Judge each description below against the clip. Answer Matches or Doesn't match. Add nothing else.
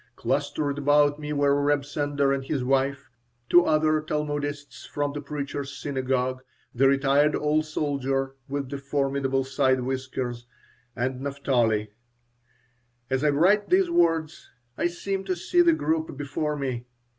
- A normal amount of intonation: Doesn't match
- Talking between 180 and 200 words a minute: Doesn't match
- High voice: Doesn't match